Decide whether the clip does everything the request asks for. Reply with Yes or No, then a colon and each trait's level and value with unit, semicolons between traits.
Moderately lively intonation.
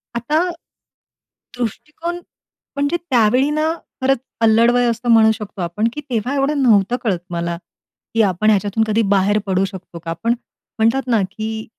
Yes: average, 4.2 semitones